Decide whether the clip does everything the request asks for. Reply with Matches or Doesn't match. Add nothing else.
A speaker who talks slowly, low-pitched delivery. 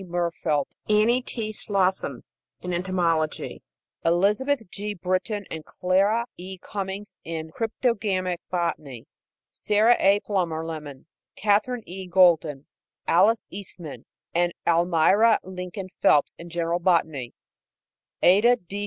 Doesn't match